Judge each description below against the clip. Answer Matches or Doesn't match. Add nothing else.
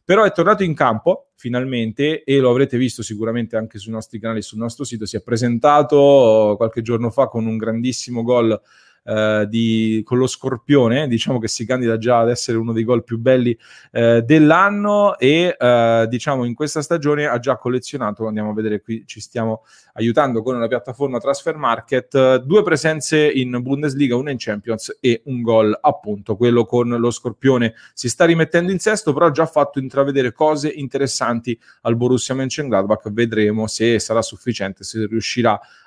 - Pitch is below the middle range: Matches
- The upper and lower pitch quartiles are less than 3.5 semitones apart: Doesn't match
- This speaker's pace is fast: Doesn't match